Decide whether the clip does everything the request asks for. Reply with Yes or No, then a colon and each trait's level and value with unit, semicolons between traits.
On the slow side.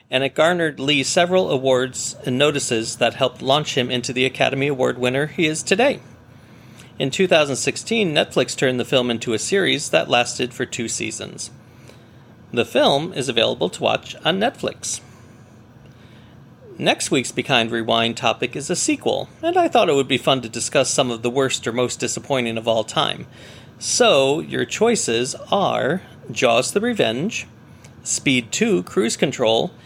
No: average, 160 wpm